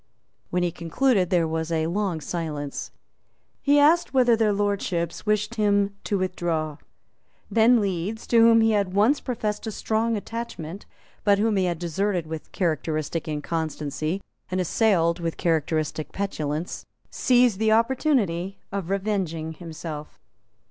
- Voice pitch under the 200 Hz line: Yes, high, 190 Hz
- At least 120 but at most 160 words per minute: Yes, slow, 135 wpm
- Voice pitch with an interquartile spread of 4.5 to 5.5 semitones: Yes, average, 5.0 semitones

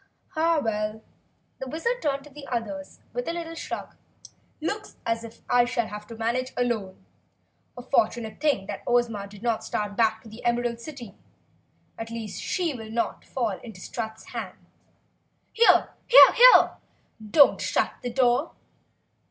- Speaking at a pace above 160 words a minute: No, average, 150 wpm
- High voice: Yes, high, 235 Hz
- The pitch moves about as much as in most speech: Yes, average, 4.0 semitones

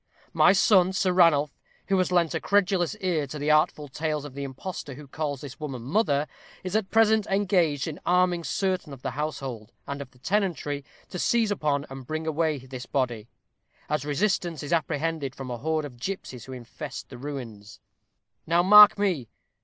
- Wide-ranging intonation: No, average, 4.8 semitones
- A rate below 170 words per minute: No, average, 185 wpm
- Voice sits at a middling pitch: Yes, medium, 155 Hz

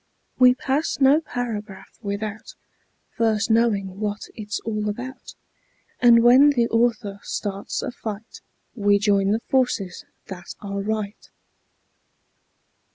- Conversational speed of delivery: No, slow, 115 wpm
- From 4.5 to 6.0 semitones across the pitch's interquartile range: No, average, 3.1 semitones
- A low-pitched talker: No, high, 215 Hz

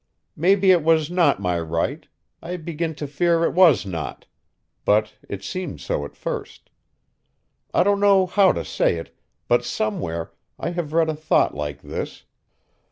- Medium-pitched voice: Yes, medium, 155 Hz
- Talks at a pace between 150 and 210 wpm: Yes, average, 165 wpm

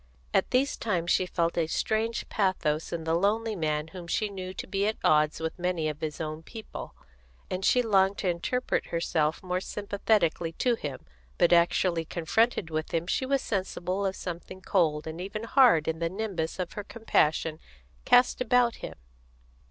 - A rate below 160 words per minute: No, average, 175 wpm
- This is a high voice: No, medium, 180 Hz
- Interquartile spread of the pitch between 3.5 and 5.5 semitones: Yes, average, 4.7 semitones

